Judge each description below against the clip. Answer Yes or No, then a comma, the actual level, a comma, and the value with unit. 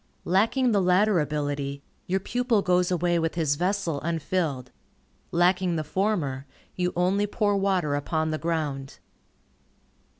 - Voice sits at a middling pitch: Yes, medium, 175 Hz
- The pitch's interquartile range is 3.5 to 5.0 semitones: Yes, average, 4.2 semitones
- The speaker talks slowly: Yes, slow, 130 wpm